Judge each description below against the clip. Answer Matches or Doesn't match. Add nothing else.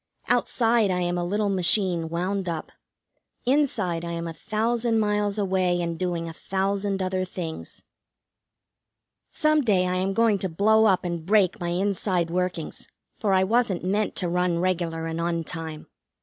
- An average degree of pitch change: Matches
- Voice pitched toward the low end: Doesn't match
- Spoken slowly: Doesn't match